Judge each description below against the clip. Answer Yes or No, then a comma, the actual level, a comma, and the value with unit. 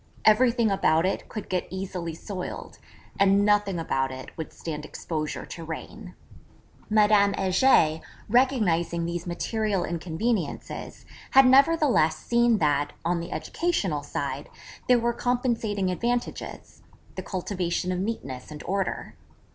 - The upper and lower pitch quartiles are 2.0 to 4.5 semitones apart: No, wide, 5.4 semitones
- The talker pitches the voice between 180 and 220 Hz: Yes, high, 190 Hz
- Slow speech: Yes, slow, 125 wpm